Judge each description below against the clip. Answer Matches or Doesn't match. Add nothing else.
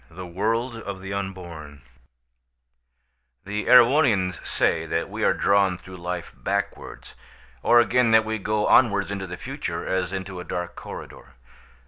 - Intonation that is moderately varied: Matches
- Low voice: Matches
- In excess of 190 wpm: Doesn't match